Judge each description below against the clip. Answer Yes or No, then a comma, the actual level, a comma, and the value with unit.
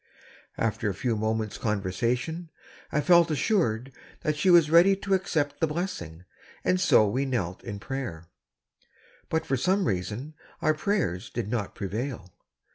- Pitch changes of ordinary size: No, wide, 8.1 semitones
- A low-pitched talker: Yes, low, 130 Hz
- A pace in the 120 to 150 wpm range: Yes, average, 145 wpm